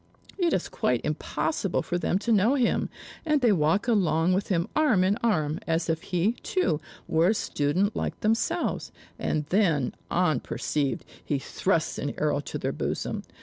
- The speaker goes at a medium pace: Yes, average, 165 wpm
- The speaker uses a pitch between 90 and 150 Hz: No, medium, 180 Hz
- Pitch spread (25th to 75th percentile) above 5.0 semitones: Yes, wide, 5.6 semitones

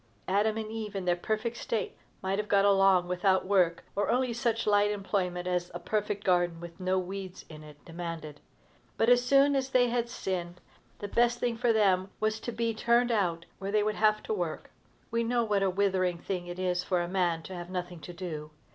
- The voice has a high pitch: Yes, high, 195 Hz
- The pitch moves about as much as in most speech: Yes, average, 3.8 semitones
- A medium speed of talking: No, fast, 215 wpm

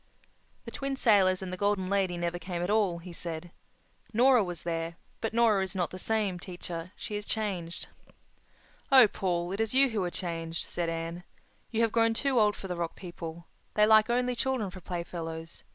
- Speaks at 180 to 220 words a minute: Yes, average, 190 wpm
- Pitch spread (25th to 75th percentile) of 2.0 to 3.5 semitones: No, average, 4.3 semitones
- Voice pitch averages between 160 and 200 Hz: Yes, medium, 185 Hz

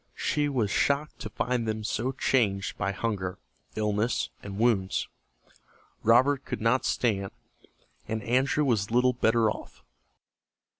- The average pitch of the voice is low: Yes, low, 115 Hz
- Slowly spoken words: Yes, slow, 130 wpm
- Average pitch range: Yes, average, 3.4 semitones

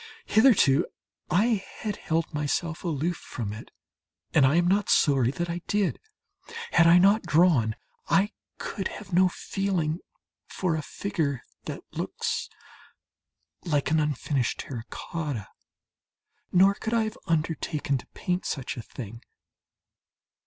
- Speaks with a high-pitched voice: No, medium, 165 Hz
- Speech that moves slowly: Yes, slow, 130 wpm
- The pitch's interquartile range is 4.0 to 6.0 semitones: Yes, average, 5.0 semitones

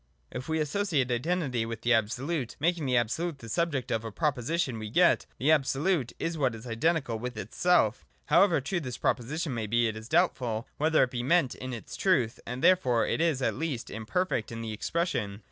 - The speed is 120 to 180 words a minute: No, average, 195 wpm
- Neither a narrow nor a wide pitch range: No, wide, 6.1 semitones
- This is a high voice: No, low, 130 Hz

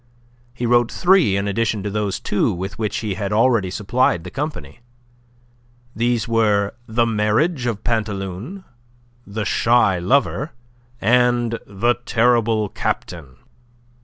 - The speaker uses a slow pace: Yes, slow, 125 wpm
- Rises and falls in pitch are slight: No, average, 3.2 semitones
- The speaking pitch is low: Yes, low, 110 Hz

